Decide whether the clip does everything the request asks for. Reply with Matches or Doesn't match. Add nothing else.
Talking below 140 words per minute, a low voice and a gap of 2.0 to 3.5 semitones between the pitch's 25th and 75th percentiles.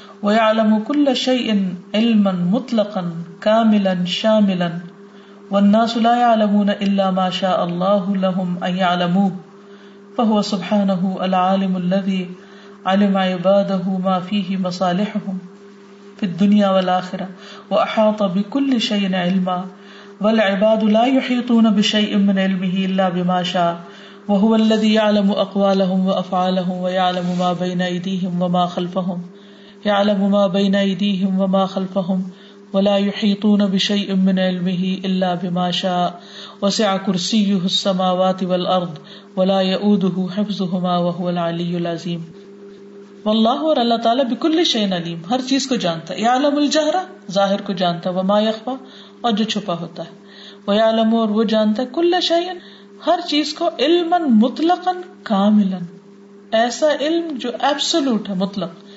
Doesn't match